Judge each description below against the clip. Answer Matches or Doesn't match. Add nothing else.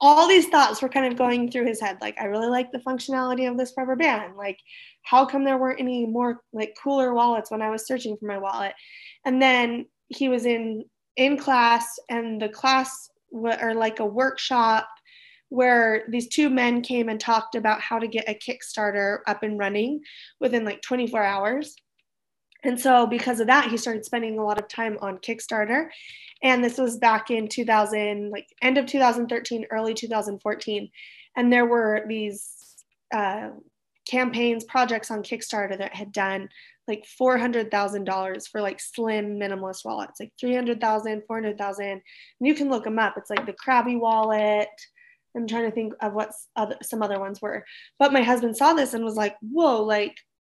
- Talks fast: Doesn't match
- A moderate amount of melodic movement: Matches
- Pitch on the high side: Matches